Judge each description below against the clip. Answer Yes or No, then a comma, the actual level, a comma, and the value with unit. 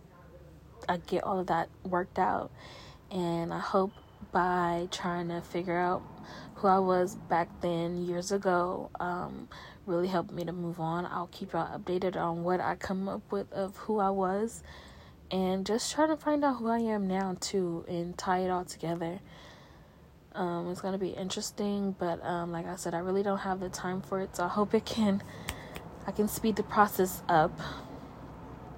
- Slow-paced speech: No, average, 185 wpm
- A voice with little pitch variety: Yes, narrow, 2.1 semitones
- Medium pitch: Yes, medium, 180 Hz